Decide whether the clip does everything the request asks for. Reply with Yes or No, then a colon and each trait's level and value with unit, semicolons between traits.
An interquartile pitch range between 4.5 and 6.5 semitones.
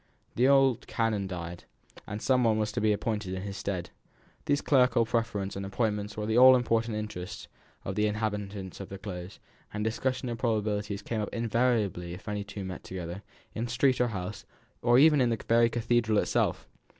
No: average, 3.1 semitones